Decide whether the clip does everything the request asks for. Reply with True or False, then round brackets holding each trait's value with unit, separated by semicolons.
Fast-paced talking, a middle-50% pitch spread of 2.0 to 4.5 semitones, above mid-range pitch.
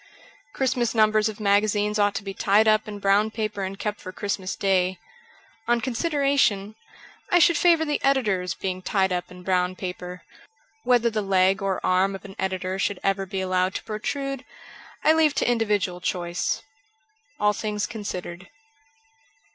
False (165 wpm; 2.8 semitones; 205 Hz)